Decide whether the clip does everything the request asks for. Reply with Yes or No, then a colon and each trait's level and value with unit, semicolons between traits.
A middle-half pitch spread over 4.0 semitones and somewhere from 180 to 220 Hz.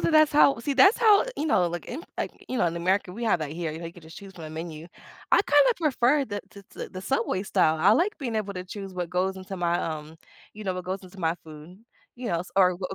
Yes: wide, 5.6 semitones; medium, 185 Hz